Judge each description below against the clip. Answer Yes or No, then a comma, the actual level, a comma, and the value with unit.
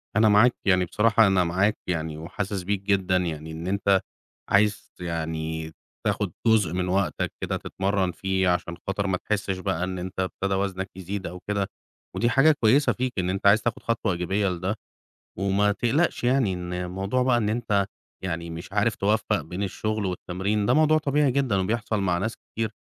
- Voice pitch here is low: Yes, low, 100 Hz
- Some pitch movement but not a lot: Yes, average, 3.0 semitones